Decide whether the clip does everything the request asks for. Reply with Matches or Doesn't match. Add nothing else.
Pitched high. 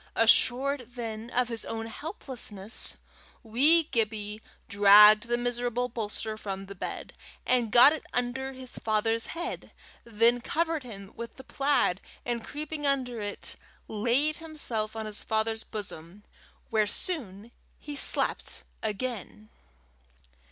Matches